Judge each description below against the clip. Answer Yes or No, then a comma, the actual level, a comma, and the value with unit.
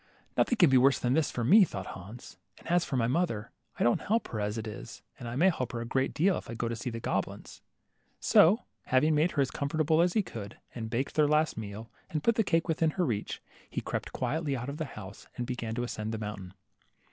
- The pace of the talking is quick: Yes, fast, 250 wpm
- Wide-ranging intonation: Yes, wide, 6.0 semitones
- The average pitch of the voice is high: No, low, 130 Hz